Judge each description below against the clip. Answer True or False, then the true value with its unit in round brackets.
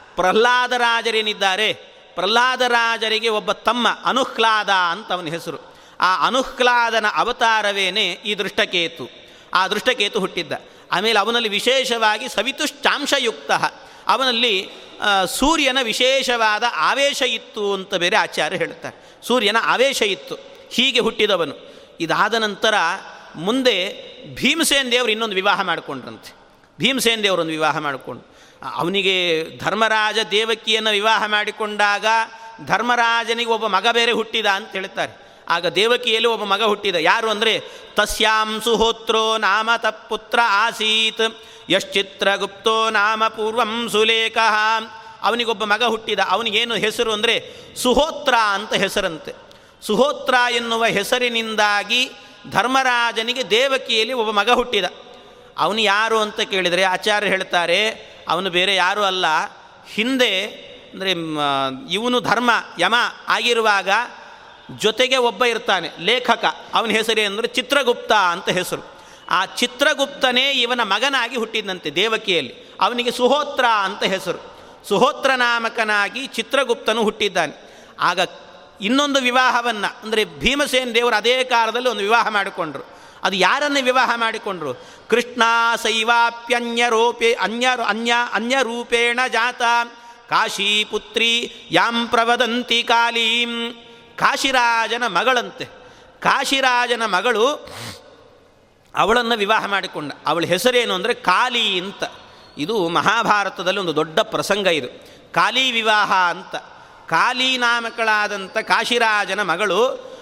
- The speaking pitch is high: True (230 Hz)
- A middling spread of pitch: True (3.0 semitones)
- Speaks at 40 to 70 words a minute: False (100 wpm)